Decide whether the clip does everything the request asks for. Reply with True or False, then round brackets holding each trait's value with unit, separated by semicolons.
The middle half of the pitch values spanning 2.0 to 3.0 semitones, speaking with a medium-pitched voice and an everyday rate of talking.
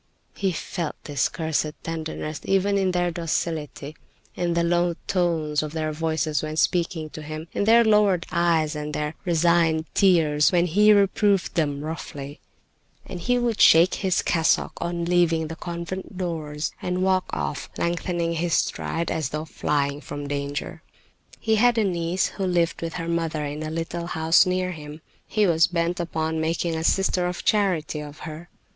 True (2.4 semitones; 165 Hz; 170 wpm)